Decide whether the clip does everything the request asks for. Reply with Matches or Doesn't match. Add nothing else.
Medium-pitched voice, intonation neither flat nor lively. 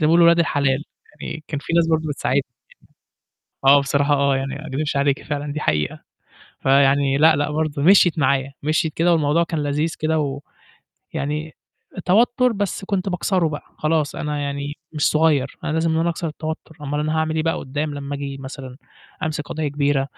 Doesn't match